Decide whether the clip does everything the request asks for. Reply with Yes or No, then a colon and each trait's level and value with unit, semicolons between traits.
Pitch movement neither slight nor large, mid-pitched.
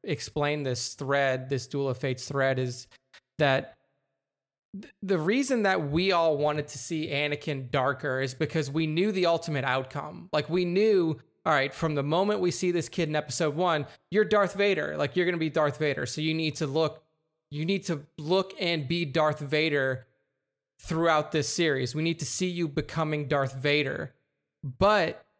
Yes: average, 3.4 semitones; medium, 155 Hz